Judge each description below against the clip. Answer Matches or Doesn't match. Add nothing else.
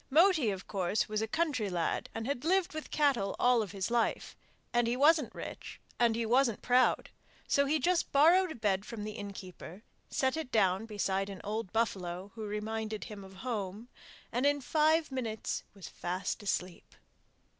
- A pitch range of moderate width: Doesn't match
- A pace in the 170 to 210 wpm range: Matches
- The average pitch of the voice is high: Matches